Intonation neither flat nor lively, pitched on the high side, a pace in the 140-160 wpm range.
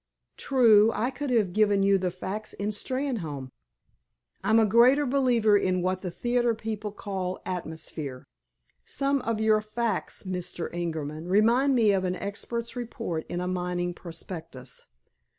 Yes: average, 4.6 semitones; high, 205 Hz; average, 145 wpm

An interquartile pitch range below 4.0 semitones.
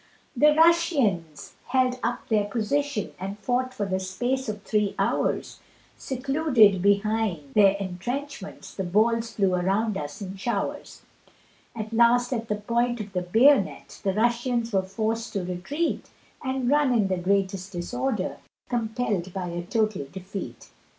No: average, 4.3 semitones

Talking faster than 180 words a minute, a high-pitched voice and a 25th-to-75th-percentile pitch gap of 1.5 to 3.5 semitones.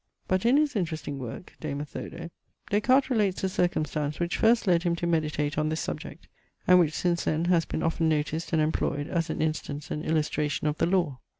No: fast, 205 wpm; medium, 165 Hz; average, 3.0 semitones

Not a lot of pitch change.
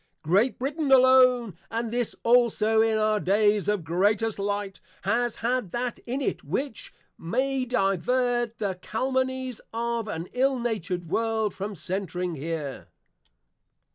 No: average, 4.1 semitones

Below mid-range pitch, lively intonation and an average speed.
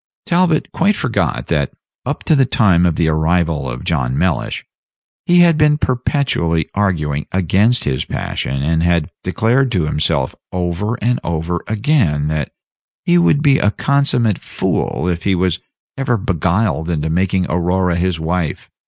Yes: very low, 90 Hz; wide, 7.2 semitones; average, 155 wpm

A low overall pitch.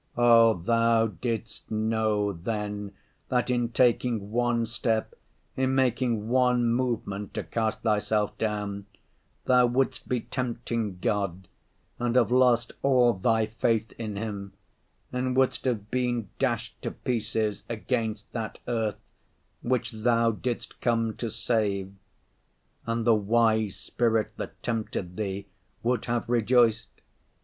Yes: low, 115 Hz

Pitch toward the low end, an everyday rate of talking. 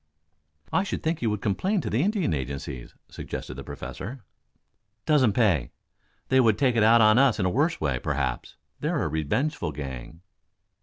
Yes: low, 110 Hz; average, 170 wpm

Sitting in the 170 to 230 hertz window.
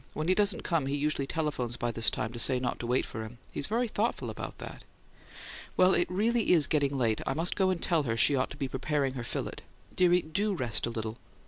No: medium, 145 Hz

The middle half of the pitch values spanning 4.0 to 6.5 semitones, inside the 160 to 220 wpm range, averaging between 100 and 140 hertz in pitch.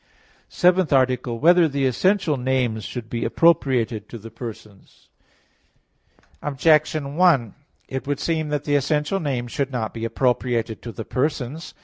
Yes: average, 4.3 semitones; average, 170 wpm; low, 135 Hz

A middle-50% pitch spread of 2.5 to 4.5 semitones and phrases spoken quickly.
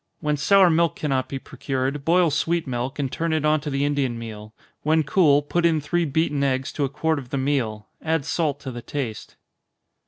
Yes: average, 3.2 semitones; fast, 210 wpm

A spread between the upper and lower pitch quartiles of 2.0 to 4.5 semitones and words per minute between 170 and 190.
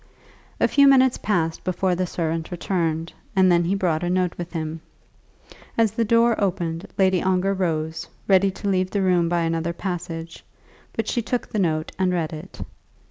Yes: average, 2.9 semitones; average, 180 wpm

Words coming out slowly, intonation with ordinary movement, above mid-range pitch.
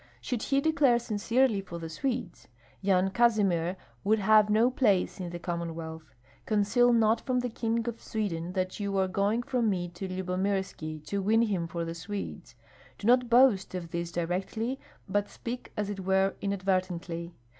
No: average, 165 wpm; average, 4.4 semitones; high, 195 Hz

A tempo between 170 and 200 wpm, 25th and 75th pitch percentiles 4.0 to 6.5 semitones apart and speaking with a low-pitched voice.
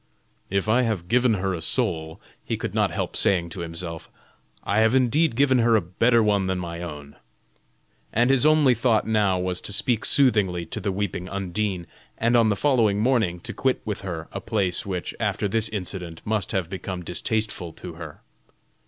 Yes: average, 190 wpm; average, 4.5 semitones; low, 100 Hz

